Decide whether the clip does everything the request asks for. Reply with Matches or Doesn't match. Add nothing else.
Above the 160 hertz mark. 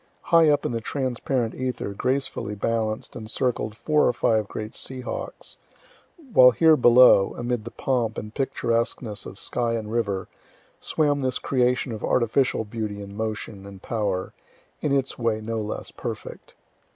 Doesn't match